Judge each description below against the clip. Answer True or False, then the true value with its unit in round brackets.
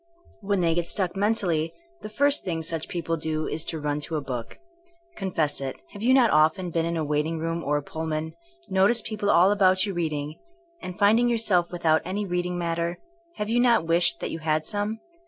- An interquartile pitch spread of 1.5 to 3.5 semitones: False (4.2 semitones)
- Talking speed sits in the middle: False (210 wpm)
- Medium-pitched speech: True (170 Hz)